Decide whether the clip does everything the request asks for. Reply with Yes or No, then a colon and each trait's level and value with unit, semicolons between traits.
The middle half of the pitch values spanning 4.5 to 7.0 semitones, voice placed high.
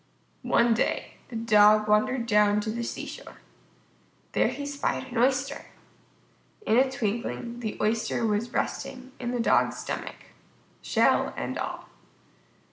No: average, 3.0 semitones; high, 235 Hz